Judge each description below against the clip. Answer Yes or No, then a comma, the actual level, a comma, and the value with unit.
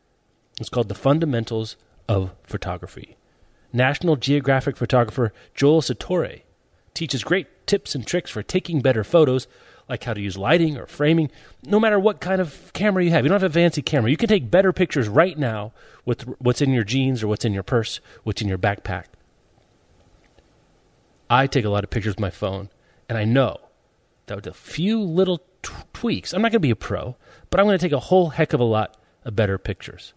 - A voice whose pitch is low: Yes, low, 130 Hz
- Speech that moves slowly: No, fast, 205 wpm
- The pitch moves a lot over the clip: Yes, wide, 7.2 semitones